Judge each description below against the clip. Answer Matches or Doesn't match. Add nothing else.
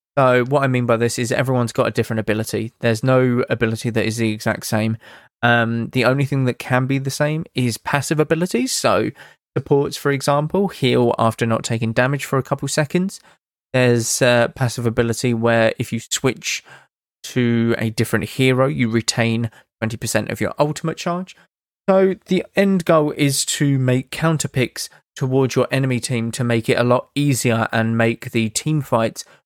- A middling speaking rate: Matches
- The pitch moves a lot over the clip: Doesn't match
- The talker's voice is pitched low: Matches